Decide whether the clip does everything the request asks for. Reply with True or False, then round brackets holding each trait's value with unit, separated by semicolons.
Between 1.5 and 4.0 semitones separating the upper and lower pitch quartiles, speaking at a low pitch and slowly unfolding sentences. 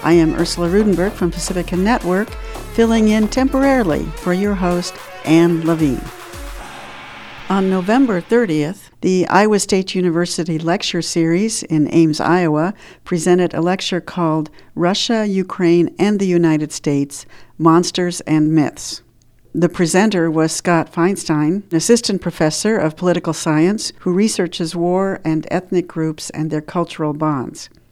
False (2.9 semitones; 175 Hz; 130 wpm)